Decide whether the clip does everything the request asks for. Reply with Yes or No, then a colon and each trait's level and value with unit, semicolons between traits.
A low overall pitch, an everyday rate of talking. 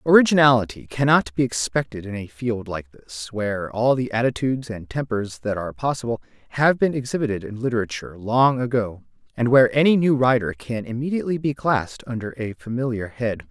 Yes: low, 120 Hz; average, 170 wpm